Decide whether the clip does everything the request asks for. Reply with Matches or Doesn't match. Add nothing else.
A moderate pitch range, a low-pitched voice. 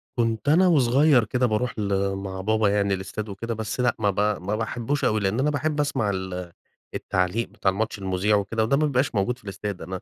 Matches